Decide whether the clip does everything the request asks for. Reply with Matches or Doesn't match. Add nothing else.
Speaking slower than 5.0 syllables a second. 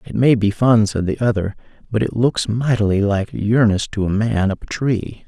Matches